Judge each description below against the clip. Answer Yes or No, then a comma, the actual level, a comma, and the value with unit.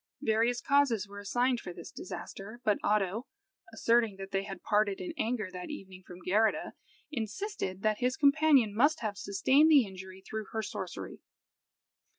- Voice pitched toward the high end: Yes, high, 215 Hz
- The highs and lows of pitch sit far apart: No, average, 4.1 semitones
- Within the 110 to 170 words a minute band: Yes, average, 160 wpm